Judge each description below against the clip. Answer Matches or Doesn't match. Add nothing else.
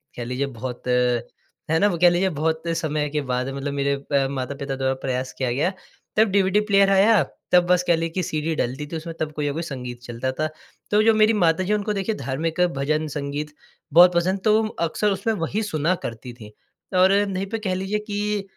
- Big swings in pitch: Matches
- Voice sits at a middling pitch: Matches